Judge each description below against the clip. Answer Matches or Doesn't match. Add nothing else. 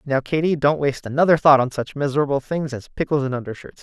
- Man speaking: Matches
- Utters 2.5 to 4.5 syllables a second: Doesn't match